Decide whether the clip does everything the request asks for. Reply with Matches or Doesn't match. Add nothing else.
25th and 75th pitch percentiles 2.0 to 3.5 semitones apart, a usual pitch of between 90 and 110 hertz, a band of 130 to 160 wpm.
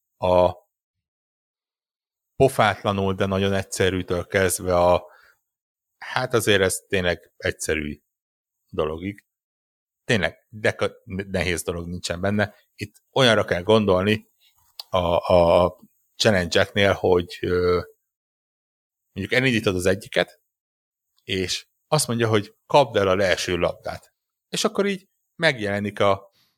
Doesn't match